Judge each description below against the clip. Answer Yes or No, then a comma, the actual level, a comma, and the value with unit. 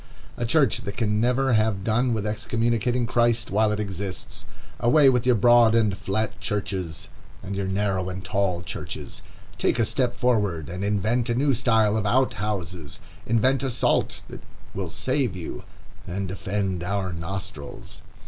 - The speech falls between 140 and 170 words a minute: Yes, average, 160 wpm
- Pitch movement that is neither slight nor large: Yes, average, 3.8 semitones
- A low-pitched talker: Yes, low, 105 Hz